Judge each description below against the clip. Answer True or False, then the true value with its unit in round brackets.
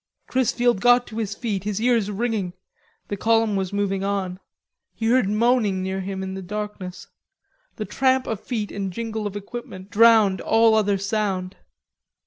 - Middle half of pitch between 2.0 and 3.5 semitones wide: True (2.9 semitones)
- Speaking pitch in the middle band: False (210 Hz)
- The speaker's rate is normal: True (160 wpm)